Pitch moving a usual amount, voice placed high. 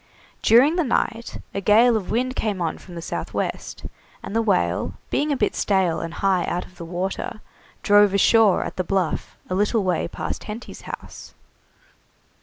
Yes: average, 3.9 semitones; high, 200 Hz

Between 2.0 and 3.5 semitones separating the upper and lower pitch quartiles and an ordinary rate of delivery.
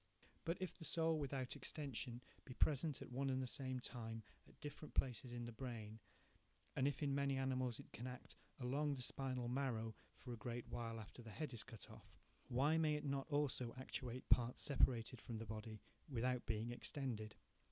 Yes: average, 2.8 semitones; average, 195 wpm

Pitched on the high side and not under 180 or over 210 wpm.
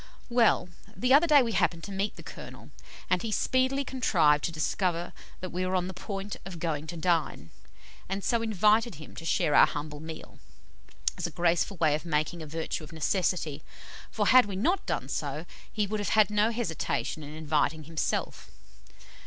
No: medium, 180 Hz; average, 185 wpm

